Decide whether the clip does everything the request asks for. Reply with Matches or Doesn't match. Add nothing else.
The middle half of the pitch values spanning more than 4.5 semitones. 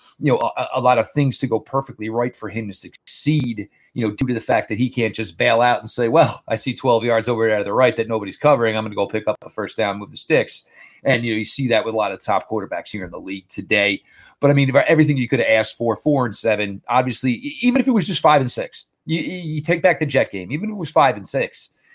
Matches